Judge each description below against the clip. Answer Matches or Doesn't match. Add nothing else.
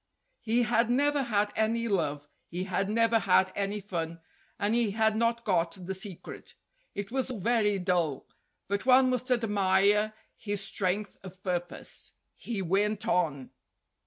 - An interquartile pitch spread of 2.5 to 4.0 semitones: Matches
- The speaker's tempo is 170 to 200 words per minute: Doesn't match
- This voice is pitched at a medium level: Doesn't match